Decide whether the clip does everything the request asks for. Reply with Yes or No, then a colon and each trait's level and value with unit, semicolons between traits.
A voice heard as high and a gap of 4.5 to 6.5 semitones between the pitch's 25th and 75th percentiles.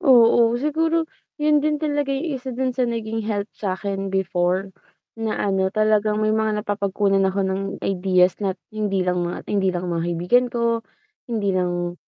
No: high, 210 Hz; average, 4.0 semitones